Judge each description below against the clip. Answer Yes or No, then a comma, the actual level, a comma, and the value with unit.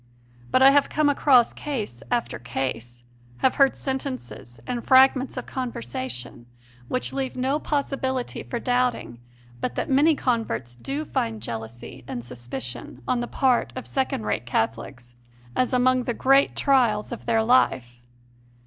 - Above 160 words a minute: No, average, 145 wpm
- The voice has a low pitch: No, high, 240 Hz